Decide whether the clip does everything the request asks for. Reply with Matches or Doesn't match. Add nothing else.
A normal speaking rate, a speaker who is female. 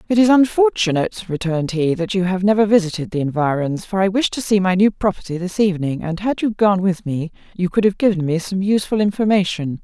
Doesn't match